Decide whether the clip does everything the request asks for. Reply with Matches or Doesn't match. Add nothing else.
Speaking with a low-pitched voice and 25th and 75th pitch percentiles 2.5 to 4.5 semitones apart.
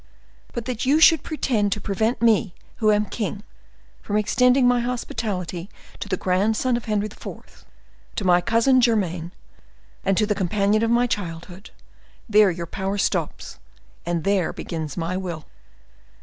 Doesn't match